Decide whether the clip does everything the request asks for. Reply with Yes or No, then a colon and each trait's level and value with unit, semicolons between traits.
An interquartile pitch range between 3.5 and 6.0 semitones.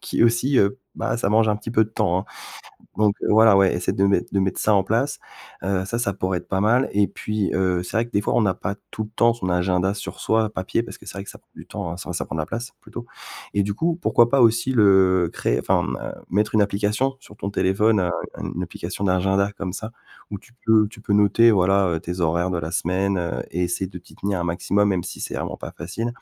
No: average, 3.1 semitones